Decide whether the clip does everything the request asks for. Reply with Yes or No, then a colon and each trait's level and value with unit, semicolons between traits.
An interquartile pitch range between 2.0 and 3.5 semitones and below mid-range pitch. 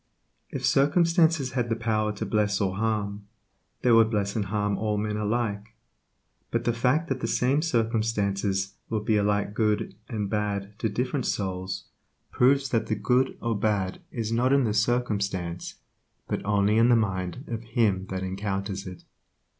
Yes: average, 2.8 semitones; low, 110 Hz